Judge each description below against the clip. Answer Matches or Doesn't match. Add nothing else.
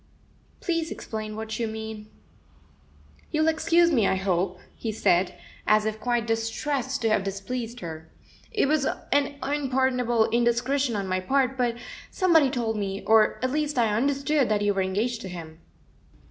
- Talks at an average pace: Matches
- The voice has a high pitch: Matches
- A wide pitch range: Doesn't match